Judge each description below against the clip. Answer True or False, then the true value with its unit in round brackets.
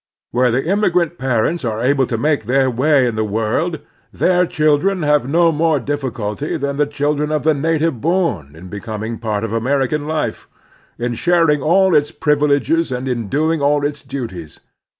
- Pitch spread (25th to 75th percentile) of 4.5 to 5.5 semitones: True (4.8 semitones)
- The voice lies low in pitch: False (145 Hz)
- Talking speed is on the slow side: False (170 wpm)